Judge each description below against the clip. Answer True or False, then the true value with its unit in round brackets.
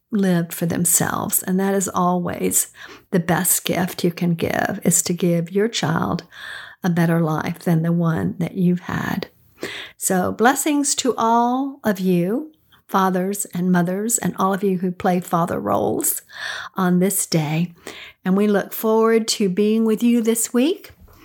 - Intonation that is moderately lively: True (3.9 semitones)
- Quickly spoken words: False (160 wpm)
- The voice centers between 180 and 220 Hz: True (190 Hz)